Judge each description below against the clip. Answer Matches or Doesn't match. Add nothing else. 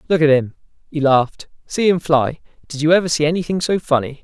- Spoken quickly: Matches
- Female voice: Doesn't match